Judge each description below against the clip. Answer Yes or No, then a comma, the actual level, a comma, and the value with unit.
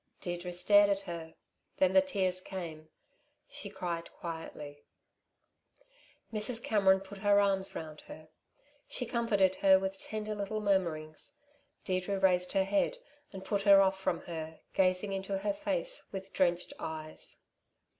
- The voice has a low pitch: No, high, 190 Hz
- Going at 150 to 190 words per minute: No, average, 140 wpm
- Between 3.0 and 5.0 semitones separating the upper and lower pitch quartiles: No, narrow, 2.5 semitones